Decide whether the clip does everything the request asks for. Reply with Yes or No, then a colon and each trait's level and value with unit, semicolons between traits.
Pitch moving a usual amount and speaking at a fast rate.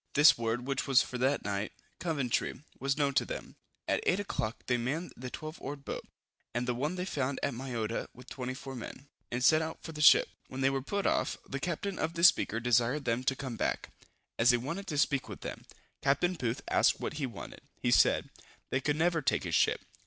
Yes: average, 3.6 semitones; fast, 220 wpm